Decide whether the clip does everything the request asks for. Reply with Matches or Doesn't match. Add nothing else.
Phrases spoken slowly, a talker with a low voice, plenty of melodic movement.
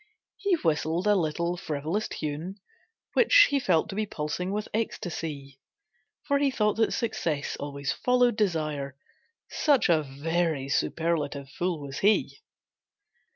Doesn't match